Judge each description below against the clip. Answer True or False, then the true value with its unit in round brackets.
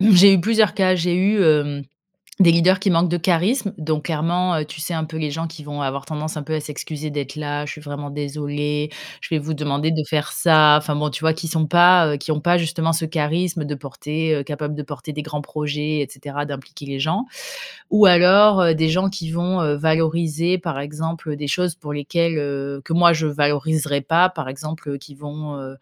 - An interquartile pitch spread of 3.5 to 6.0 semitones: False (2.5 semitones)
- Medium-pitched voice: True (155 Hz)